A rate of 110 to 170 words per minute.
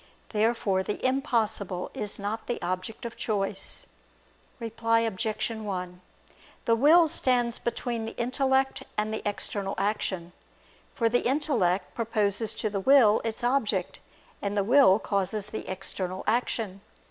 Yes: slow, 135 wpm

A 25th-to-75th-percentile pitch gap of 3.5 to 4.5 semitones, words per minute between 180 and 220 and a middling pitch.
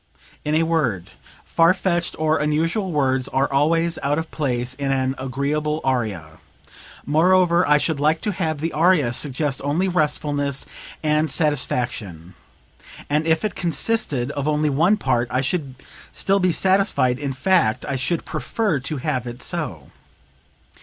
No: average, 4.0 semitones; average, 150 wpm; medium, 150 Hz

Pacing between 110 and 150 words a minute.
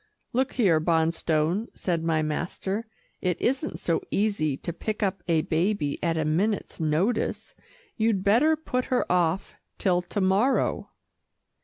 Yes: average, 140 wpm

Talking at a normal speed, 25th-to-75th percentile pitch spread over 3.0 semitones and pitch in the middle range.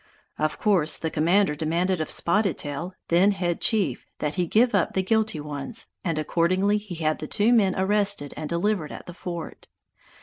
Yes: average, 180 wpm; average, 4.6 semitones; medium, 180 Hz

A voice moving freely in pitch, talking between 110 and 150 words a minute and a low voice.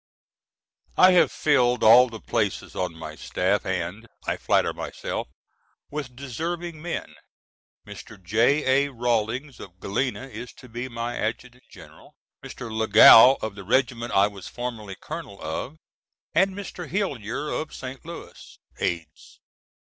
No: average, 4.9 semitones; slow, 135 wpm; low, 120 Hz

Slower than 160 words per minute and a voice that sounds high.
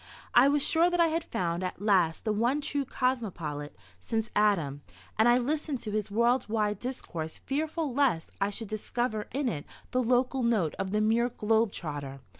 No: average, 180 wpm; high, 225 Hz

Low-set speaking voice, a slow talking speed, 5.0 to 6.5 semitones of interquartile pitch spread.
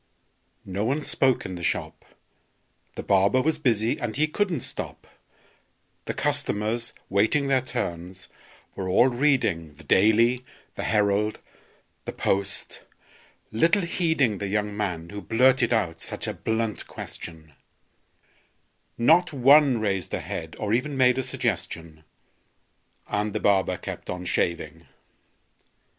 Yes: low, 110 Hz; slow, 130 wpm; wide, 5.5 semitones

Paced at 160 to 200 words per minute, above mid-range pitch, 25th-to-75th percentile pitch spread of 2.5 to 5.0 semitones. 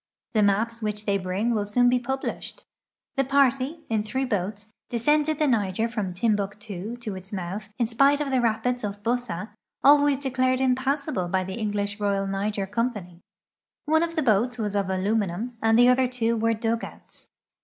Yes: average, 175 wpm; high, 225 Hz; average, 3.8 semitones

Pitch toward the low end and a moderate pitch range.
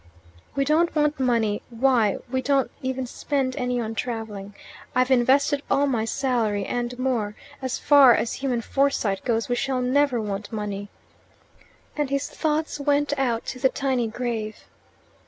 No: very high, 250 Hz; average, 3.4 semitones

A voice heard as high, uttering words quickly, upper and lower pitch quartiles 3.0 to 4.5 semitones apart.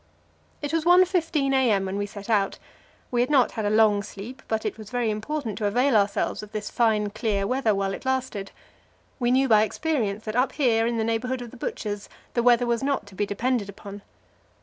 Yes: high, 225 Hz; fast, 215 wpm; average, 3.8 semitones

